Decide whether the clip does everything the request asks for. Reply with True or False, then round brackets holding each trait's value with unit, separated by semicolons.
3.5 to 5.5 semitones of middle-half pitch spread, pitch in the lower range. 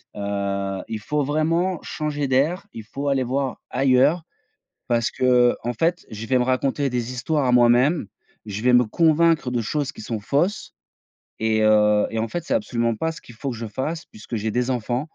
True (4.7 semitones; 125 Hz)